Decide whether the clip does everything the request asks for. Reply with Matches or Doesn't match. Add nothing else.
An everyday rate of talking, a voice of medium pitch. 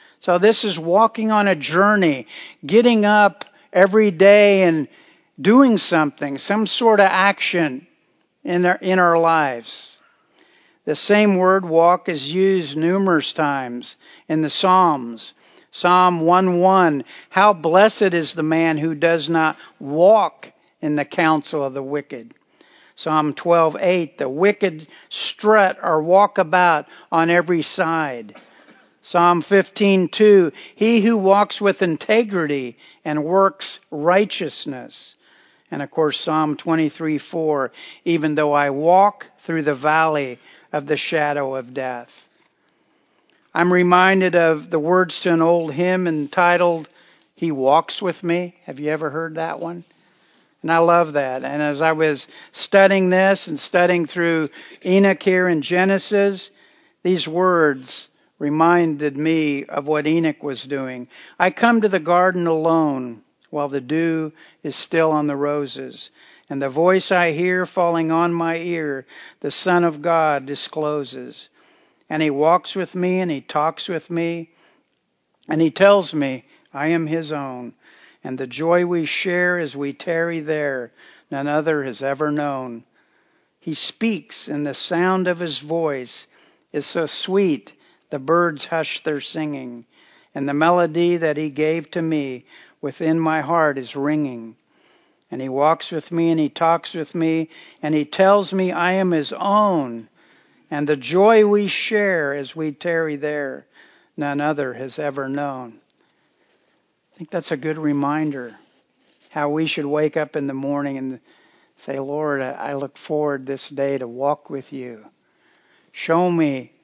Matches